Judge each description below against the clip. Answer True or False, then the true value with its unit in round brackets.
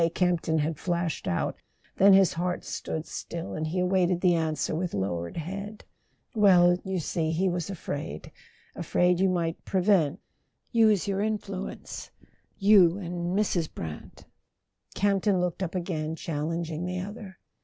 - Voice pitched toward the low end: False (180 Hz)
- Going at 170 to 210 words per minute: False (150 wpm)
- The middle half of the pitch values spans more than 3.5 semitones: False (2.9 semitones)